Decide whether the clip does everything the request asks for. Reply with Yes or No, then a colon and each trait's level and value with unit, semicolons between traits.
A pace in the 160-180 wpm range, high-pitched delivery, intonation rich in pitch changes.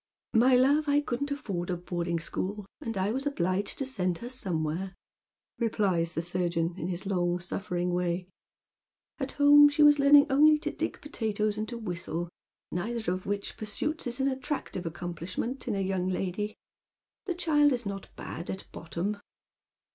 Yes: average, 175 wpm; high, 205 Hz; wide, 7.1 semitones